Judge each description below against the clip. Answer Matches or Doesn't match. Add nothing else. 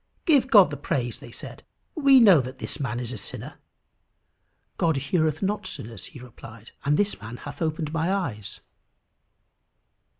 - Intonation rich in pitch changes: Matches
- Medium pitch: Matches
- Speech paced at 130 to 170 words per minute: Matches